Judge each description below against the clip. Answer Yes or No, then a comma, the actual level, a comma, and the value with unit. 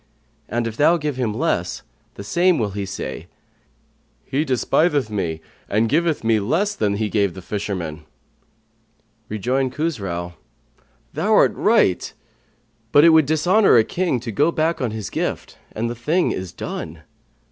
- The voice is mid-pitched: No, low, 120 Hz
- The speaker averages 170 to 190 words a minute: No, average, 150 wpm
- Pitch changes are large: Yes, wide, 7.4 semitones